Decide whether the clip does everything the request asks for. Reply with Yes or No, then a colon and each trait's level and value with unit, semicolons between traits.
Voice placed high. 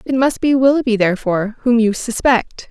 Yes: high, 235 Hz